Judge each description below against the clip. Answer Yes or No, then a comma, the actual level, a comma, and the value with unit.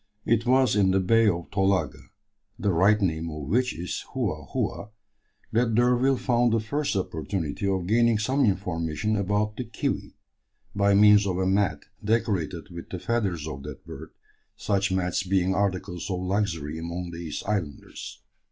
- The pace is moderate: Yes, average, 160 wpm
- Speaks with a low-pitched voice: Yes, low, 100 Hz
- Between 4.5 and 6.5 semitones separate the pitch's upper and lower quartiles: No, average, 3.6 semitones